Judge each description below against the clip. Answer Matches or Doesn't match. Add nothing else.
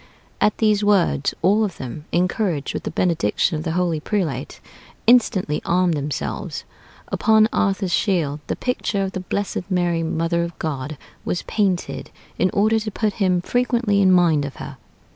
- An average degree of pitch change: Matches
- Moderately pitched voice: Matches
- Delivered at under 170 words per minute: Matches